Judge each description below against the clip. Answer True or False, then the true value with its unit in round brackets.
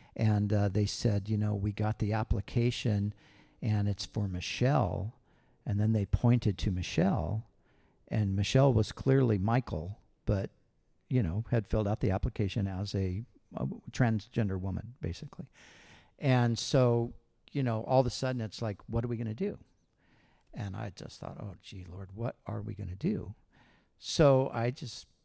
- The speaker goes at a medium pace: True (170 wpm)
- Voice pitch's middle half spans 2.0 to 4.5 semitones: True (2.9 semitones)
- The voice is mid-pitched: False (110 Hz)